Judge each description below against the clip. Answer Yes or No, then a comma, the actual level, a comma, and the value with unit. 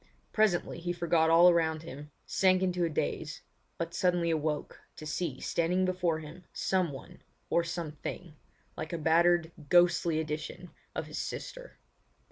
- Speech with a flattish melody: Yes, narrow, 2.0 semitones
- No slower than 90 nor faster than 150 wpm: Yes, average, 140 wpm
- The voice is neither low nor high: Yes, medium, 170 Hz